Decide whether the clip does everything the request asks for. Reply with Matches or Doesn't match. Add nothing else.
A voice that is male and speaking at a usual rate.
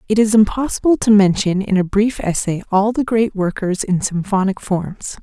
Doesn't match